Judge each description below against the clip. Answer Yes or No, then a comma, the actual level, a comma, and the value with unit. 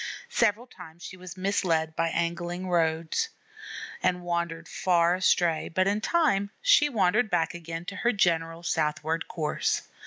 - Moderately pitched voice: Yes, medium, 175 Hz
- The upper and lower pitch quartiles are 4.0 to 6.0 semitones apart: No, average, 3.0 semitones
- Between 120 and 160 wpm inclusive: Yes, average, 145 wpm